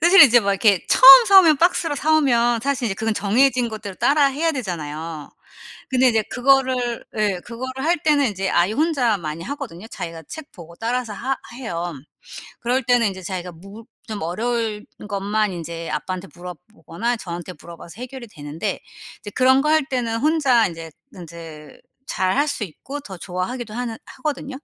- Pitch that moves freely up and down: Yes, wide, 6.3 semitones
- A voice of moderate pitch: No, high, 225 Hz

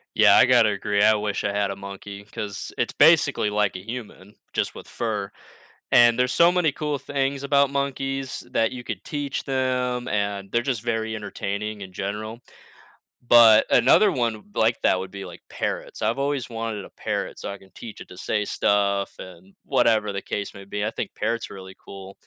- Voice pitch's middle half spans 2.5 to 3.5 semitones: No, average, 4.0 semitones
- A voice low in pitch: Yes, low, 110 Hz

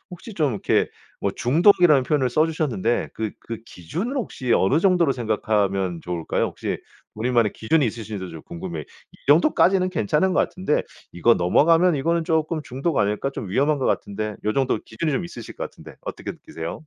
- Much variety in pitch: Yes, wide, 7.5 semitones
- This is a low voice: Yes, low, 130 Hz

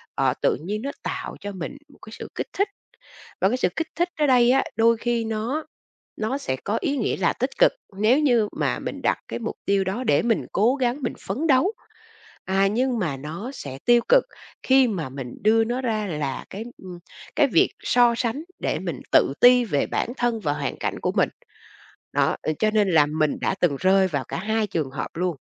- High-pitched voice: Yes, high, 220 Hz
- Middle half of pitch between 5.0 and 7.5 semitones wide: Yes, wide, 5.5 semitones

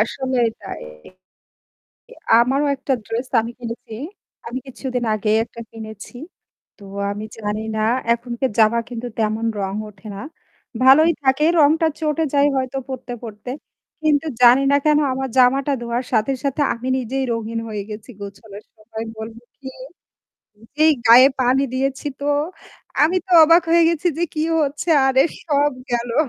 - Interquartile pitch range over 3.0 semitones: Yes, average, 3.7 semitones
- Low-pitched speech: No, very high, 250 Hz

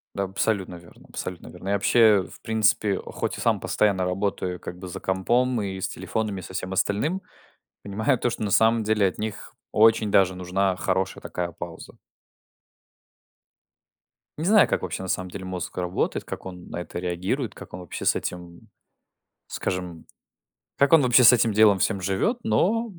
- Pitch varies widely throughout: No, average, 3.3 semitones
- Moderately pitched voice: No, low, 100 Hz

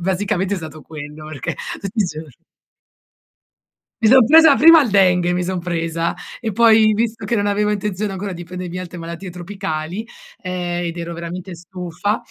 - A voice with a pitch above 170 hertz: Yes, medium, 185 Hz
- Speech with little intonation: No, average, 3.4 semitones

